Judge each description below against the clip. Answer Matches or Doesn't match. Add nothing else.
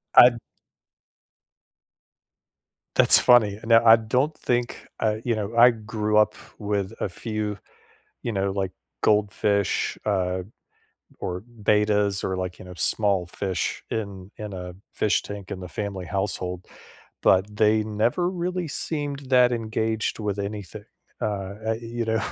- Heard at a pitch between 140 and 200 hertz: Doesn't match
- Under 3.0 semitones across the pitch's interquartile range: Matches